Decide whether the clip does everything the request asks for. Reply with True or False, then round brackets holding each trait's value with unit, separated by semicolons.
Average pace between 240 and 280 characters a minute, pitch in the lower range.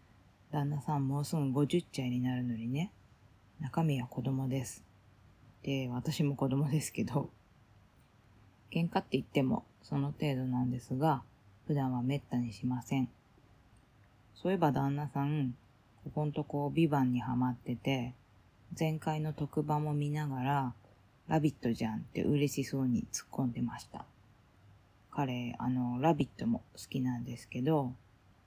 True (275 characters per minute; 130 Hz)